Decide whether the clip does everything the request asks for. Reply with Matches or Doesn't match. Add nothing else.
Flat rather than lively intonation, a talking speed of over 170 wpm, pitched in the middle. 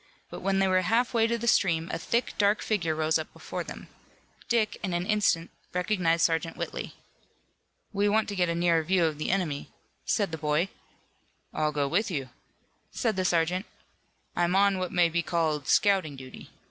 Doesn't match